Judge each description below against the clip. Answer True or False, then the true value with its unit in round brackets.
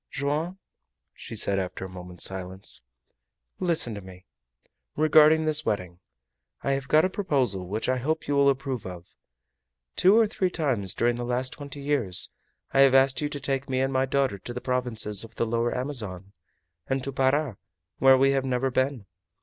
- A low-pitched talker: True (130 Hz)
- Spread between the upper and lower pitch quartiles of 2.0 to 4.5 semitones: False (5.1 semitones)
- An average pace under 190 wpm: True (180 wpm)